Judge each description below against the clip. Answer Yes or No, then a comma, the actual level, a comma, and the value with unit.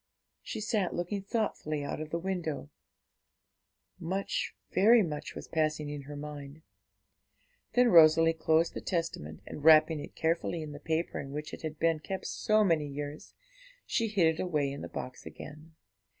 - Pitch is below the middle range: No, medium, 160 Hz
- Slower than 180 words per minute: Yes, average, 165 wpm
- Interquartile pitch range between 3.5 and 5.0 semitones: No, average, 2.8 semitones